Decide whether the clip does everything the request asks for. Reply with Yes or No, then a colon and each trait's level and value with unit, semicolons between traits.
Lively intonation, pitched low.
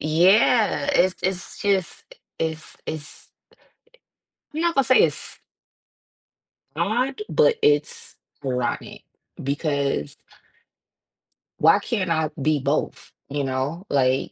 No: wide, 6.0 semitones; medium, 160 Hz